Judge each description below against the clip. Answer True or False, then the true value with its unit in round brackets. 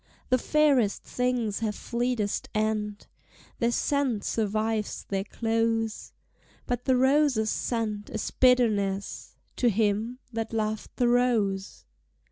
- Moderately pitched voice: False (225 Hz)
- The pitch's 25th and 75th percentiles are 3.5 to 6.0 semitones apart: False (2.8 semitones)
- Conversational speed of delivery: False (110 wpm)